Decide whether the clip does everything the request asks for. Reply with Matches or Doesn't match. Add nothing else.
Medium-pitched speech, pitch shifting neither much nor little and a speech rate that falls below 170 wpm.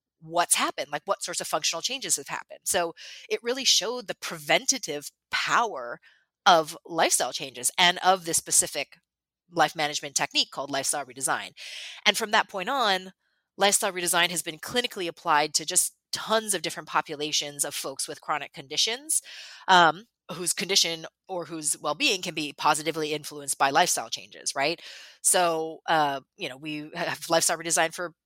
Matches